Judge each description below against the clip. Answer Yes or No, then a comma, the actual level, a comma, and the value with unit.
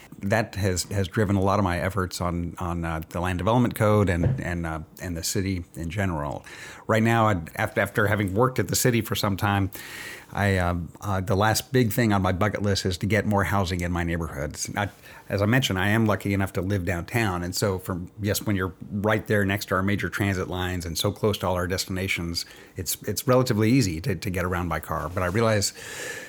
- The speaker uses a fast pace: Yes, fast, 230 wpm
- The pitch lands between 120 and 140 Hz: No, low, 100 Hz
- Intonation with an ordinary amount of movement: Yes, average, 3.0 semitones